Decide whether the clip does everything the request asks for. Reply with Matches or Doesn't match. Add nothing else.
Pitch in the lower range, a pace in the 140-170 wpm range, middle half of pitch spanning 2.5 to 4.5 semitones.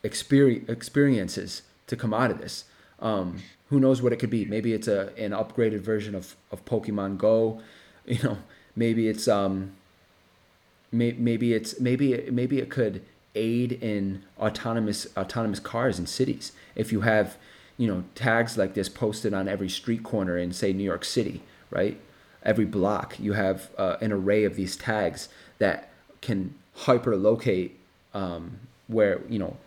Matches